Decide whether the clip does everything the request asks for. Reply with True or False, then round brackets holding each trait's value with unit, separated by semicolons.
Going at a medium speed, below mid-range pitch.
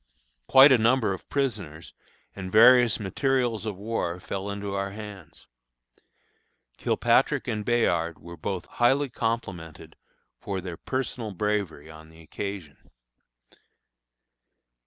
False (115 wpm; 100 Hz)